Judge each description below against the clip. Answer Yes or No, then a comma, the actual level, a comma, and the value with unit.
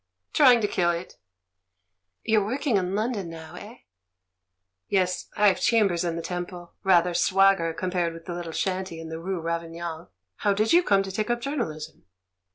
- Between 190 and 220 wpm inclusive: No, average, 165 wpm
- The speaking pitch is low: No, medium, 185 Hz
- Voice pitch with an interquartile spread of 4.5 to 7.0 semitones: No, average, 3.6 semitones